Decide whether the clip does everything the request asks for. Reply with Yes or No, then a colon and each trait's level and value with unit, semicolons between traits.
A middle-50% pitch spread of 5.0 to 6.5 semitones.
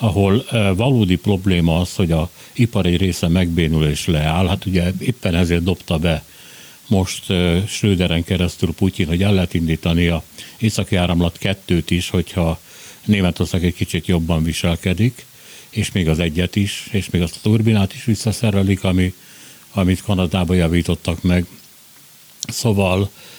No: average, 2.7 semitones